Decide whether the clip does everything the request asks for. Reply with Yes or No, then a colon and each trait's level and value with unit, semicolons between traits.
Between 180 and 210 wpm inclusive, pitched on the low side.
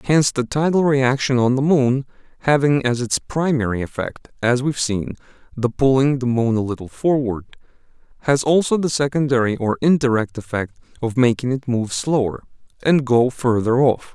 No: average, 165 wpm; low, 130 Hz